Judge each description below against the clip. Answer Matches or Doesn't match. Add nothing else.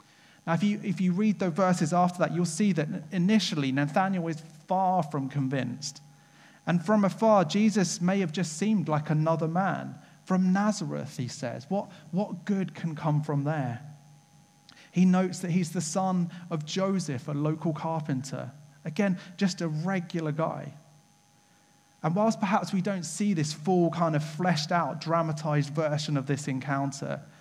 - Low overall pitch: Doesn't match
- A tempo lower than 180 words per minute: Matches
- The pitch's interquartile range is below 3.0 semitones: Doesn't match